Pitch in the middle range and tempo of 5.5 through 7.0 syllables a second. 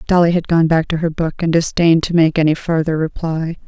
Yes: medium, 165 Hz; 5.8 syllables/s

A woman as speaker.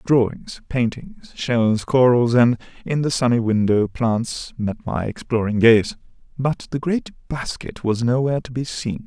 No: male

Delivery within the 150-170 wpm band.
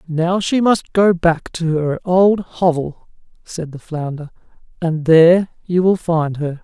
Yes: average, 165 wpm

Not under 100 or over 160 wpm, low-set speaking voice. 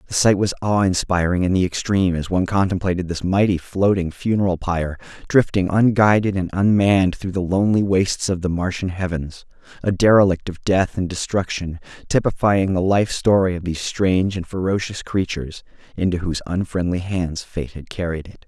No: average, 170 wpm; very low, 95 Hz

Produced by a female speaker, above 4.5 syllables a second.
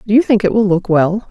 Yes: female; 6.0 syllables/s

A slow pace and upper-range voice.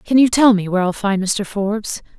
No: fast, 245 wpm; high, 210 Hz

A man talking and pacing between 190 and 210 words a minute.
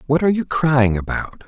Yes: male; fast, 205 wpm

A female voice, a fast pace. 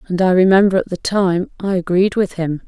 Yes: female; fast, 225 wpm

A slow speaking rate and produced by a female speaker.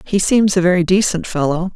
No: fast, 205 wpm; female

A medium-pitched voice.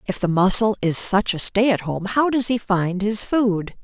No: high, 205 Hz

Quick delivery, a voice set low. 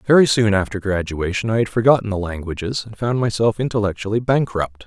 No: average, 175 wpm; low, 105 Hz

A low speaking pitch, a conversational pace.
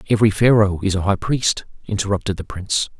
Yes: low, 100 Hz; average, 180 wpm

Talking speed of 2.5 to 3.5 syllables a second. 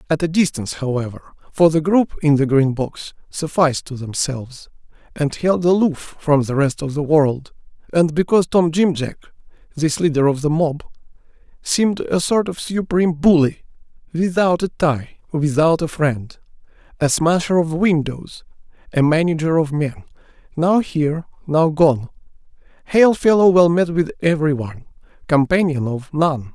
No: 4.9 syllables/s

